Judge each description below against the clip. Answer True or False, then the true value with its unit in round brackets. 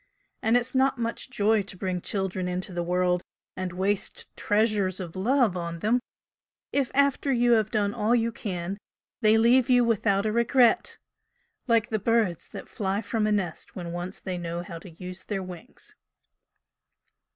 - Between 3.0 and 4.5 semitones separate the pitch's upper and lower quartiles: True (4.2 semitones)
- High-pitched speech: True (205 Hz)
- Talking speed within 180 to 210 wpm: False (170 wpm)